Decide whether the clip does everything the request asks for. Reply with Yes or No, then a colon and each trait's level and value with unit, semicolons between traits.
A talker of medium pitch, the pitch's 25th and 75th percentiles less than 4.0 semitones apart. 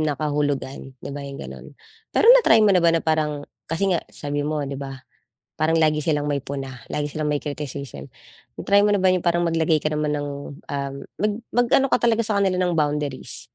Yes: medium, 150 Hz; average, 3.3 semitones